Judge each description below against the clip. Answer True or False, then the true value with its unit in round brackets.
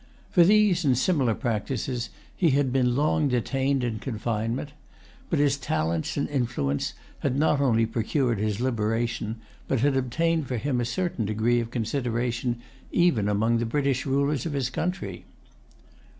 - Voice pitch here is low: True (125 Hz)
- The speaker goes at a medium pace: True (150 wpm)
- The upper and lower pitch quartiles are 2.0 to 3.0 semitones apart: False (3.7 semitones)